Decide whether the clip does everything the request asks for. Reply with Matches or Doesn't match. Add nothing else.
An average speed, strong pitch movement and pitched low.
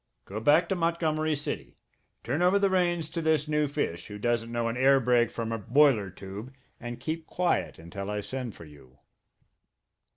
Matches